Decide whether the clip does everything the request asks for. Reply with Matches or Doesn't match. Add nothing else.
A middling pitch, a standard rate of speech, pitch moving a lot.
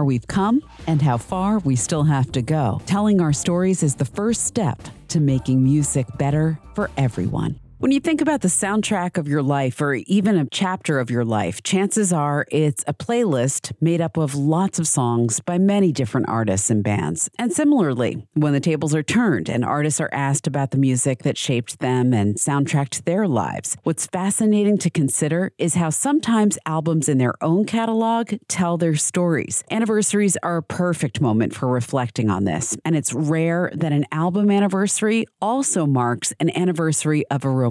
Matches